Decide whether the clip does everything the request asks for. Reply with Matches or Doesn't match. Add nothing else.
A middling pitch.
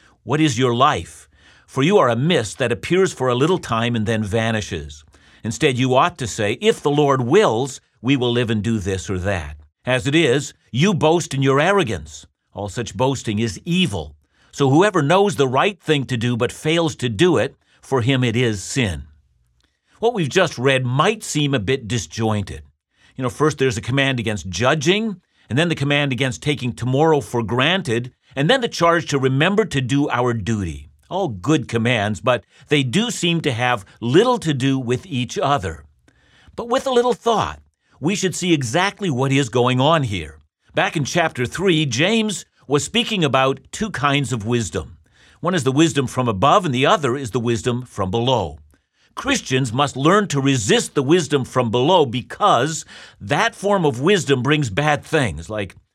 Doesn't match